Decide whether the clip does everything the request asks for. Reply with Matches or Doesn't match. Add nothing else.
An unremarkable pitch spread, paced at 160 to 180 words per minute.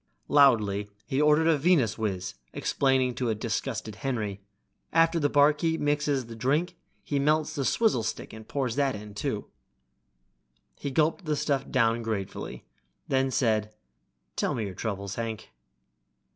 Doesn't match